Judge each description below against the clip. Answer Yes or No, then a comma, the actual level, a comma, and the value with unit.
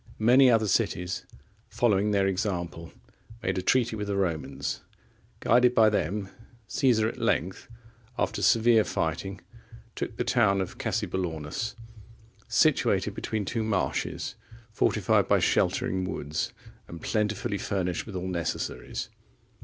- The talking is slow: Yes, slow, 120 wpm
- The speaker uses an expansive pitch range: No, average, 3.6 semitones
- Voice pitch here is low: Yes, low, 100 Hz